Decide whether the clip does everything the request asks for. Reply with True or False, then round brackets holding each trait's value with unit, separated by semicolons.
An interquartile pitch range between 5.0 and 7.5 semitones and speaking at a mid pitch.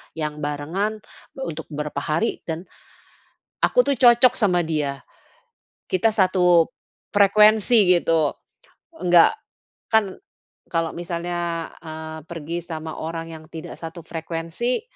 False (3.6 semitones; 170 Hz)